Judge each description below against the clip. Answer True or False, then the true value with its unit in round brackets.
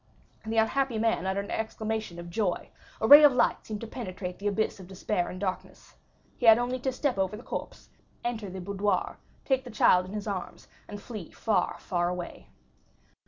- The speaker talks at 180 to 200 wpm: True (195 wpm)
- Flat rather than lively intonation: False (3.5 semitones)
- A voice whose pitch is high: True (210 Hz)